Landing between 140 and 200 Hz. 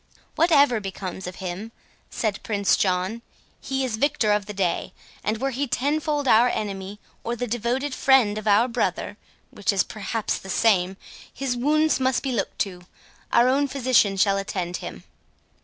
No: high, 220 Hz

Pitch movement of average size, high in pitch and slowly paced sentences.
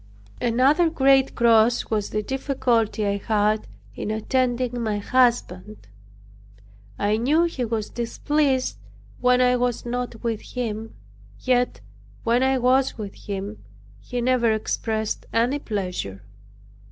Yes: average, 3.0 semitones; high, 235 Hz; slow, 120 wpm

